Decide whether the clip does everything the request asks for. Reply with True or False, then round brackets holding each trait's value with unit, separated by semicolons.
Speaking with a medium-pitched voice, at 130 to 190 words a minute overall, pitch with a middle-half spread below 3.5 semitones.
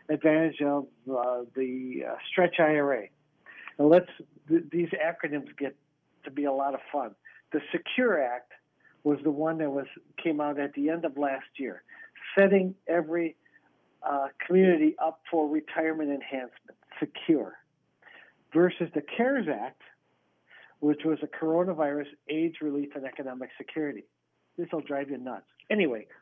True (150 Hz; 140 wpm; 2.9 semitones)